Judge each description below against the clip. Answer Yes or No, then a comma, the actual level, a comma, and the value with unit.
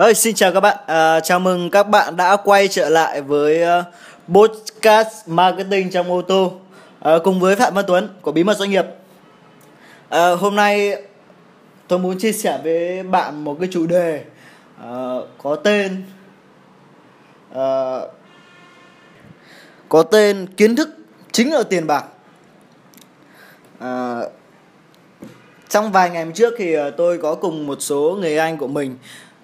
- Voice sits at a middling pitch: Yes, medium, 180 Hz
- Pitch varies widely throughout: No, average, 4.0 semitones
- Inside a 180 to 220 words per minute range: No, average, 145 wpm